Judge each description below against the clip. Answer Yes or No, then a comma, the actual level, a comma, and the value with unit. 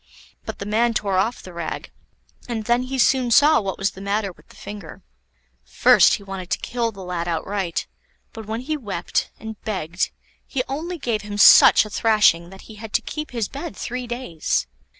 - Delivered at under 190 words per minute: No, average, 195 wpm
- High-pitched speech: Yes, high, 215 Hz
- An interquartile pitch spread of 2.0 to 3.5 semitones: No, average, 3.9 semitones